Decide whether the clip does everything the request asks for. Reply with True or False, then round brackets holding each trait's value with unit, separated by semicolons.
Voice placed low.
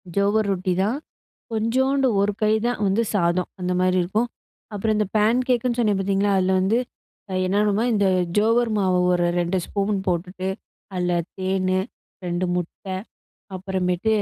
False (195 Hz)